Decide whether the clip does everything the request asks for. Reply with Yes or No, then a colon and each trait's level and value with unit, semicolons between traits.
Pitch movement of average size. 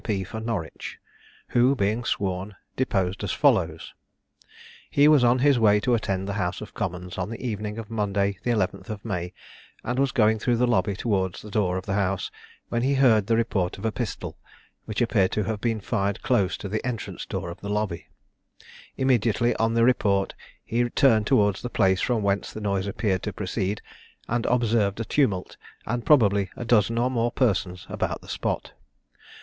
Yes: average, 3.4 semitones